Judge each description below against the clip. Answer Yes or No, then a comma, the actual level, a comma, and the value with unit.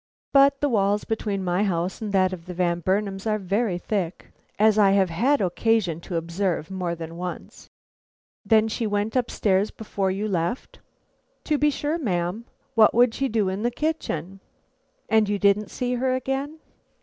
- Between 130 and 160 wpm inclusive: No, average, 175 wpm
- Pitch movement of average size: Yes, average, 3.9 semitones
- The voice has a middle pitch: No, high, 205 Hz